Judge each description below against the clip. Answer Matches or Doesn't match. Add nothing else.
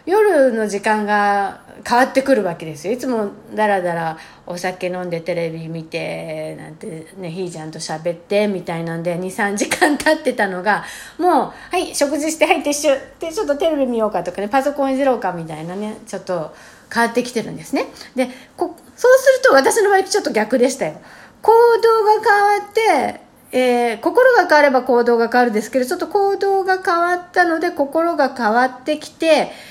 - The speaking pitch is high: Matches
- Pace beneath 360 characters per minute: Doesn't match